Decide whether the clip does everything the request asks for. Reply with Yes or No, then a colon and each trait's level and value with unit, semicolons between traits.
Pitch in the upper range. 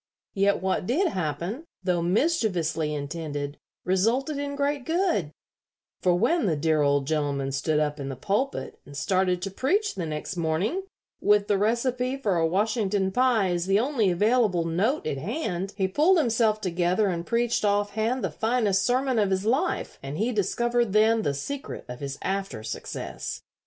Yes: high, 200 Hz